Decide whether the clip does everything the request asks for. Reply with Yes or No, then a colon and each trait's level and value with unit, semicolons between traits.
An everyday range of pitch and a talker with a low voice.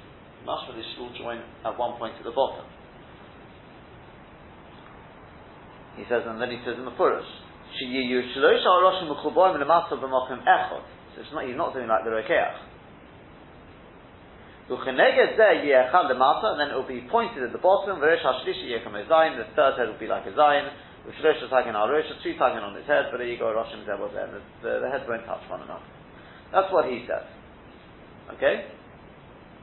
Yes: average, 5.0 semitones; low, 130 Hz